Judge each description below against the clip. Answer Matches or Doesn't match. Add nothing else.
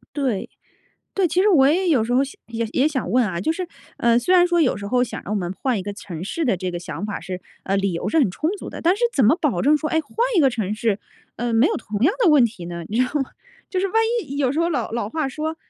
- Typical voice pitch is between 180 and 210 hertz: Doesn't match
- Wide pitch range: Matches